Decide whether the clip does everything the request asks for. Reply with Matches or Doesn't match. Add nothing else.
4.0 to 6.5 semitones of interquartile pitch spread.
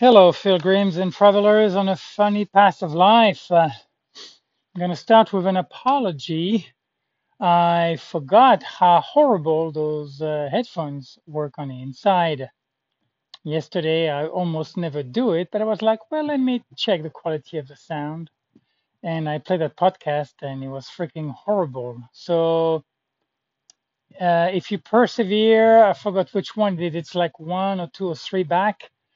Matches